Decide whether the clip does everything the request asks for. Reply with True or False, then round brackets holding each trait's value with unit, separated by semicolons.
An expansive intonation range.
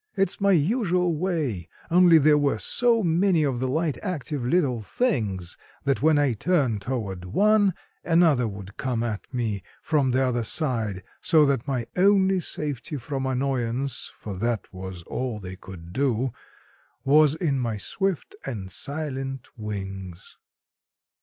True (6.7 semitones)